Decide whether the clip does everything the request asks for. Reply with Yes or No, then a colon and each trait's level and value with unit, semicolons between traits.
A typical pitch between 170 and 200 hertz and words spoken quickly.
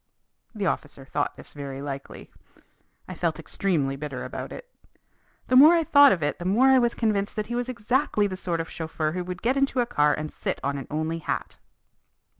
Yes: medium, 185 Hz; fast, 210 wpm